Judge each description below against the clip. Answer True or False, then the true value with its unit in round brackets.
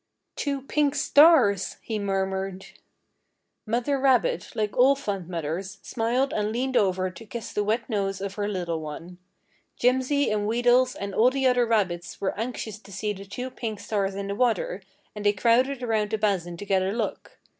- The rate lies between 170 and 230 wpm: True (180 wpm)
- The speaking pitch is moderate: False (210 Hz)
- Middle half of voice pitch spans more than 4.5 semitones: False (4.2 semitones)